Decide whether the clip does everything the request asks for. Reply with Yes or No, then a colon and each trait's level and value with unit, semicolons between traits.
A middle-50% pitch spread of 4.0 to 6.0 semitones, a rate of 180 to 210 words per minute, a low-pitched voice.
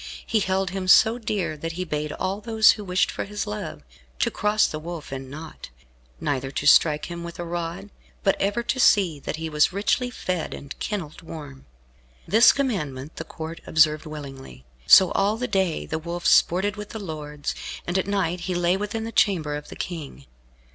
No: average, 4.9 semitones; average, 195 wpm; medium, 175 Hz